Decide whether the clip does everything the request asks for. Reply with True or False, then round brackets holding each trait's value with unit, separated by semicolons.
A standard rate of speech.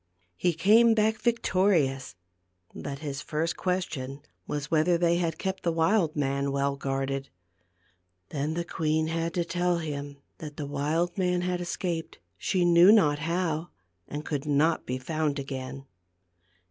True (155 wpm)